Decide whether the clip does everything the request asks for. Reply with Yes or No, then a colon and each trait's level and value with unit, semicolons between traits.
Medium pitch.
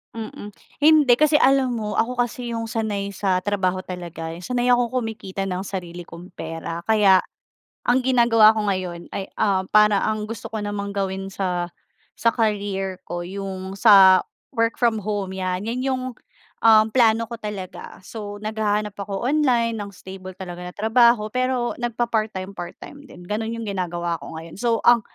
No: high, 205 Hz